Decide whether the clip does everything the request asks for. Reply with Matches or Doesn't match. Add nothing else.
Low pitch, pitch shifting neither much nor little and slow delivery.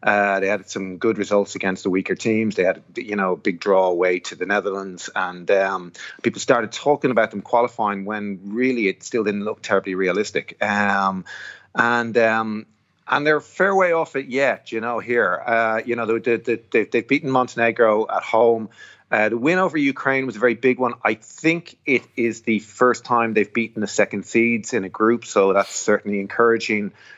Doesn't match